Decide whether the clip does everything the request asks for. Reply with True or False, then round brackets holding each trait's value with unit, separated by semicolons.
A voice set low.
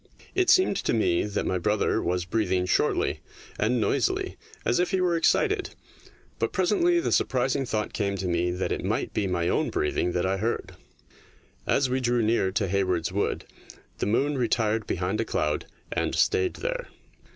True (110 Hz)